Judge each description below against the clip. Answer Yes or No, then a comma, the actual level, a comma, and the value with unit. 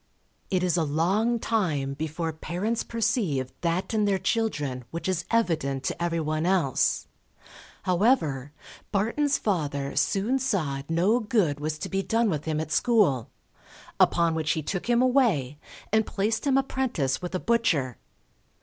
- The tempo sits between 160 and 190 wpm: No, average, 150 wpm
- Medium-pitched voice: Yes, medium, 175 Hz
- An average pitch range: No, wide, 6.7 semitones